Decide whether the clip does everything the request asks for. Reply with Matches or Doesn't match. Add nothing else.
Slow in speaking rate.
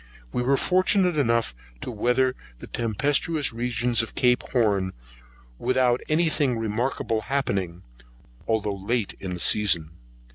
Matches